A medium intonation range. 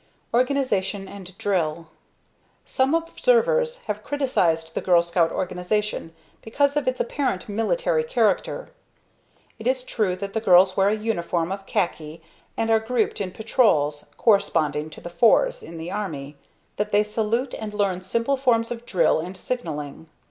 No: wide, 6.1 semitones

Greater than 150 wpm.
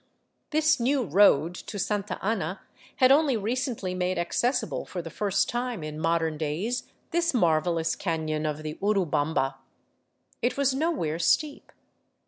No: slow, 135 wpm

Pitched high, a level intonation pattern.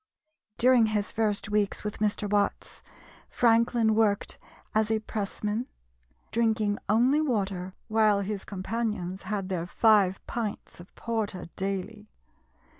Yes: high, 210 Hz; narrow, 2.1 semitones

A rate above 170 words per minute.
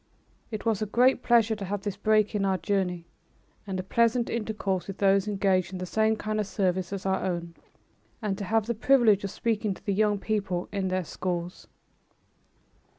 Yes: average, 195 wpm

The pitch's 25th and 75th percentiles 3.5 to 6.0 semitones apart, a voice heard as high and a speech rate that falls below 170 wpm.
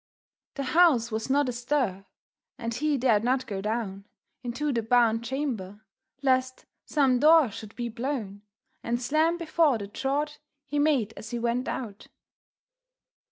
Yes: average, 4.2 semitones; high, 245 Hz; average, 145 wpm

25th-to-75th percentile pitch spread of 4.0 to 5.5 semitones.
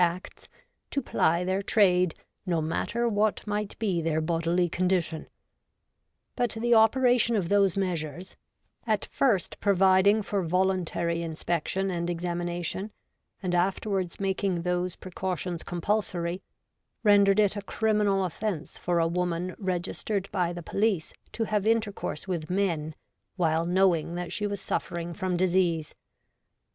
No: average, 2.9 semitones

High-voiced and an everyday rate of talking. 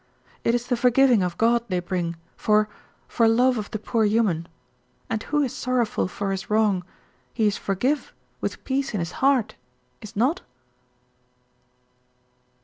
Yes: high, 225 Hz; average, 150 wpm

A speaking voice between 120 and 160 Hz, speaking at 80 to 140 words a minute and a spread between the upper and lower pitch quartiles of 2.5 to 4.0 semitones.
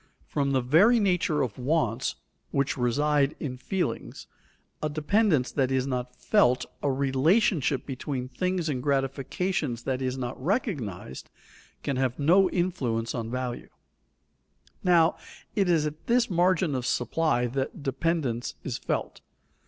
No: medium, 140 Hz; slow, 135 wpm; average, 5.0 semitones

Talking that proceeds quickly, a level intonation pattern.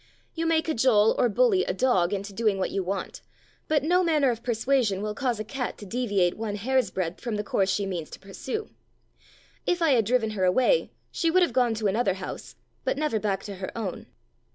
No: fast, 215 wpm; average, 5.3 semitones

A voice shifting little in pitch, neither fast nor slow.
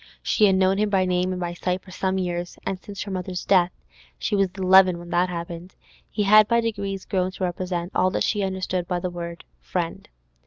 No: narrow, 1.6 semitones; fast, 220 wpm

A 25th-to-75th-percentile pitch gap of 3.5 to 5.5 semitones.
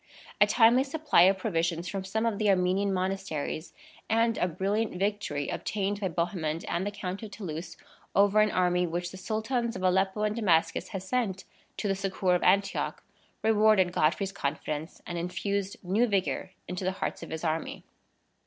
No: average, 2.9 semitones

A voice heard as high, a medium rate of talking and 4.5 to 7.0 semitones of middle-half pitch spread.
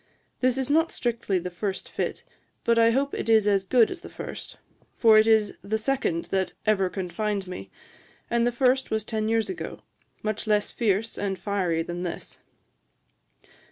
No: high, 215 Hz; average, 175 wpm; average, 3.4 semitones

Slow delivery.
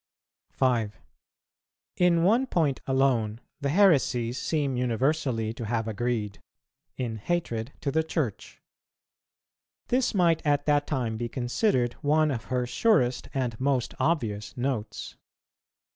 Yes: slow, 120 wpm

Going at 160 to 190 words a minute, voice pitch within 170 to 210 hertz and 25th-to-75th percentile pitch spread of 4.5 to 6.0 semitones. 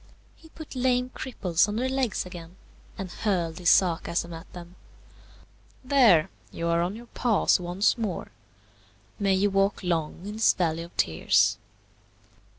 No: average, 150 wpm; medium, 185 Hz; average, 4.8 semitones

